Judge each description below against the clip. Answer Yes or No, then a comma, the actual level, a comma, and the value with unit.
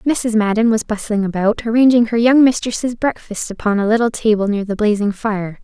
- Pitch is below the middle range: No, high, 220 Hz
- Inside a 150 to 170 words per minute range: No, average, 190 wpm